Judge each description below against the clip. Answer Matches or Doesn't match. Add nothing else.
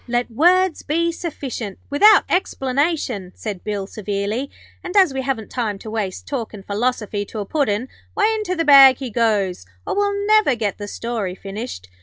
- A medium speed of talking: Matches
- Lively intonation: Matches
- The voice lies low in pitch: Doesn't match